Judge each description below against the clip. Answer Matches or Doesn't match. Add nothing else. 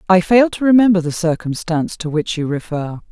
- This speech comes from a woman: Matches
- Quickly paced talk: Doesn't match